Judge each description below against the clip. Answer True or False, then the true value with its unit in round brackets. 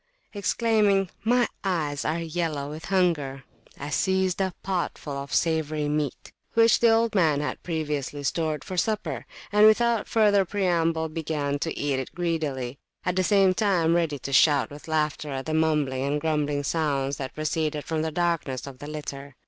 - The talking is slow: False (175 wpm)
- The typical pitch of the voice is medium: True (160 Hz)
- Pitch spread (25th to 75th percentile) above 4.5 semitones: False (4.2 semitones)